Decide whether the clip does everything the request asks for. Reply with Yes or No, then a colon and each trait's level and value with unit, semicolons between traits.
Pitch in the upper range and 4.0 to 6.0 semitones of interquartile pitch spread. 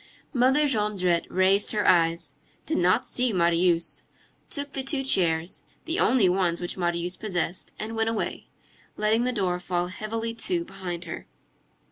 Yes: high, 195 Hz; average, 4.7 semitones